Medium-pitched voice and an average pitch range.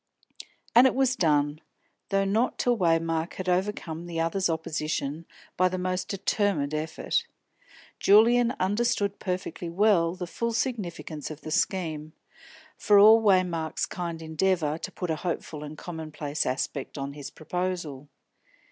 Yes: medium, 175 Hz; average, 4.0 semitones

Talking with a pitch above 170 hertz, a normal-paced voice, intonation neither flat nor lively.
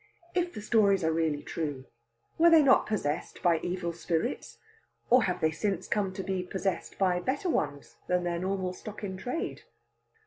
Yes: medium, 185 Hz; average, 175 wpm; average, 3.9 semitones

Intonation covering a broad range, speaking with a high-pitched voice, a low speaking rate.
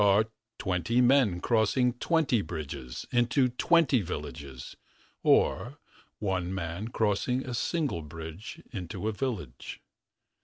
No: wide, 6.8 semitones; low, 105 Hz; slow, 115 wpm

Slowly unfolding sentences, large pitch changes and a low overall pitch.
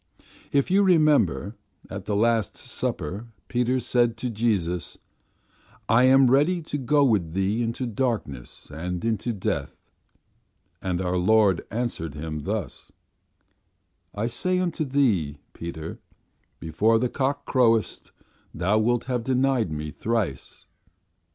Yes: slow, 125 wpm; wide, 6.2 semitones; low, 115 Hz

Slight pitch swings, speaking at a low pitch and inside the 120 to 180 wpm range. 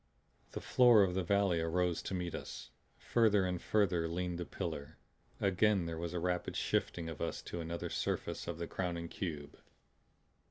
Yes: narrow, 2.3 semitones; very low, 90 Hz; average, 170 wpm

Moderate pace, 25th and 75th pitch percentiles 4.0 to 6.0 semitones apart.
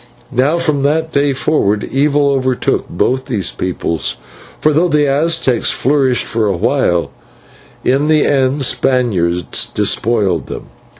No: slow, 130 wpm; average, 4.8 semitones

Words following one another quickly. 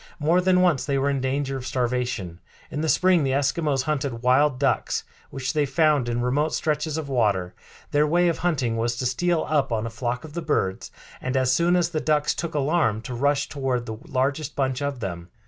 Yes: fast, 215 wpm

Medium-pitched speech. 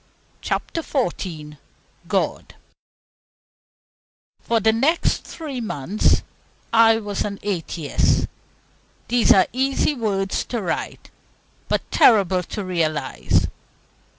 No: high, 205 Hz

